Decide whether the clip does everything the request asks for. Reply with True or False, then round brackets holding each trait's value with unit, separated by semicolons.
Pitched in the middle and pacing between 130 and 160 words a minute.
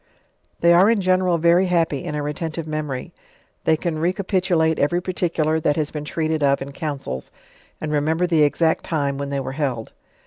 False (160 Hz; 180 wpm)